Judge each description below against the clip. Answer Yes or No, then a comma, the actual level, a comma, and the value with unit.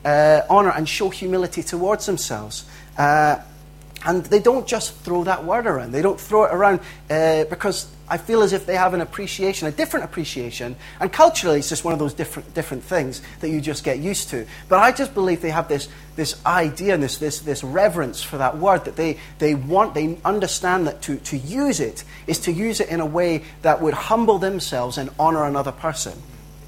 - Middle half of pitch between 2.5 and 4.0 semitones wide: No, average, 4.4 semitones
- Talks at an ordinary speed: No, fast, 210 wpm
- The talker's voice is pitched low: No, medium, 165 Hz